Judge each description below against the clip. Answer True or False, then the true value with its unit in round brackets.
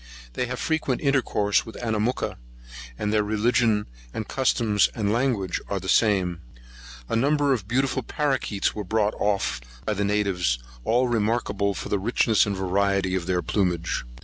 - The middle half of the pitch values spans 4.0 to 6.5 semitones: False (3.5 semitones)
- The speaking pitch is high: False (105 Hz)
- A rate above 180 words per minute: False (150 wpm)